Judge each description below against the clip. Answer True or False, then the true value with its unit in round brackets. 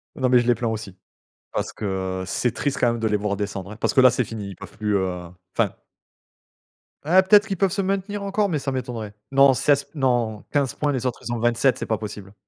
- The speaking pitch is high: False (120 Hz)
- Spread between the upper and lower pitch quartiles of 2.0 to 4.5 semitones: False (5.0 semitones)